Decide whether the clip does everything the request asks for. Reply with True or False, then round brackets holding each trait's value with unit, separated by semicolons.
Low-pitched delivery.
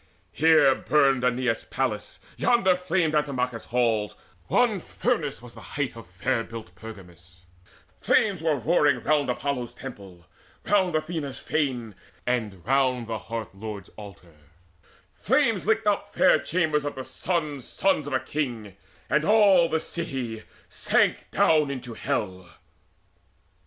True (130 Hz)